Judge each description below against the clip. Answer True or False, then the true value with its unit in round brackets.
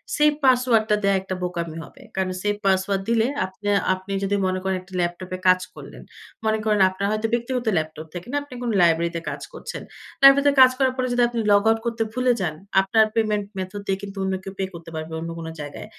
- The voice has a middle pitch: False (200 Hz)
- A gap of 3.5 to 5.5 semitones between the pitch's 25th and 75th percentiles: True (3.9 semitones)